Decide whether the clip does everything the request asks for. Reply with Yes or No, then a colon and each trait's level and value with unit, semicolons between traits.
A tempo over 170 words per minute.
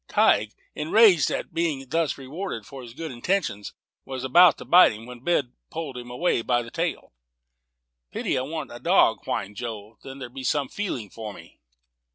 Yes: average, 185 wpm